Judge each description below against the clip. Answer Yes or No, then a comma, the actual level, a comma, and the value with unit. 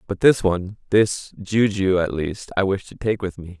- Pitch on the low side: Yes, very low, 95 Hz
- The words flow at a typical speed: No, fast, 215 wpm